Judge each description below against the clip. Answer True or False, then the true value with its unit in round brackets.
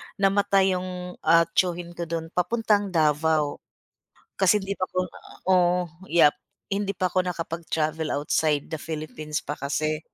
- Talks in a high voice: False (170 Hz)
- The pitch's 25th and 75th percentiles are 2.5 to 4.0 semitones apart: True (3.0 semitones)